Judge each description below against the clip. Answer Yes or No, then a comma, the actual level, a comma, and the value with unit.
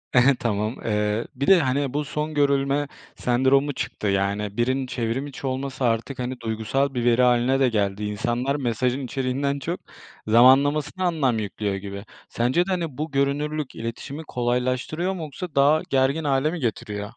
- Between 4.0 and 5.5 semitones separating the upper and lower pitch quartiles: No, average, 3.5 semitones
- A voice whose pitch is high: No, low, 130 Hz